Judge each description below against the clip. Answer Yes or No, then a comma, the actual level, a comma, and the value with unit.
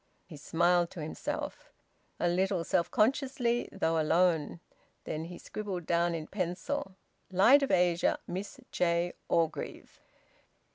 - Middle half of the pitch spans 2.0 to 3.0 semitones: Yes, narrow, 2.5 semitones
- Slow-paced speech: Yes, slow, 125 wpm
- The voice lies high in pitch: No, medium, 175 Hz